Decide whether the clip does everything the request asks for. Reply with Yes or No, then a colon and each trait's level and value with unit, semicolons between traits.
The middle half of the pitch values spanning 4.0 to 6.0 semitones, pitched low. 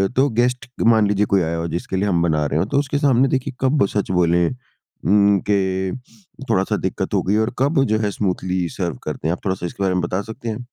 Yes: average, 4.7 semitones; low, 100 Hz